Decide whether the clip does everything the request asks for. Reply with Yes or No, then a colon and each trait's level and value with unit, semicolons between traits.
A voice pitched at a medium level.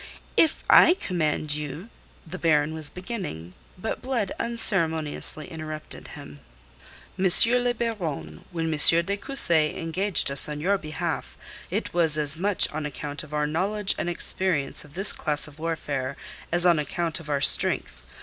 Yes: medium, 160 Hz